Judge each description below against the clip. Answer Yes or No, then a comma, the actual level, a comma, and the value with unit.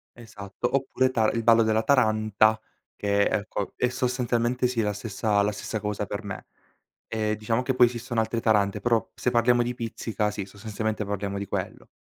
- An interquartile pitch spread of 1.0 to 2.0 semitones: No, narrow, 2.4 semitones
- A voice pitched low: Yes, low, 110 Hz